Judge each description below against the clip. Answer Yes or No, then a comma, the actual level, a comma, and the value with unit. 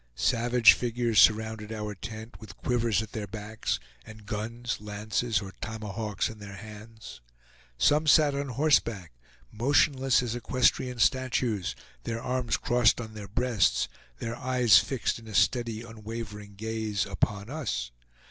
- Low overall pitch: Yes, low, 110 Hz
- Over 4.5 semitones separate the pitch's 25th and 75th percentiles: No, narrow, 2.6 semitones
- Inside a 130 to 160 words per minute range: Yes, average, 140 wpm